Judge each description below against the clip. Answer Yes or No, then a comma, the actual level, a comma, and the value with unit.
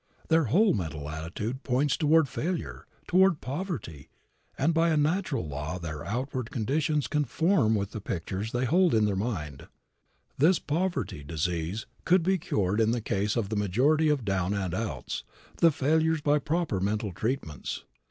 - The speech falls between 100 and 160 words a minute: Yes, average, 155 wpm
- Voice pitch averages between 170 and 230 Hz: No, low, 120 Hz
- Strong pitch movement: Yes, wide, 8.4 semitones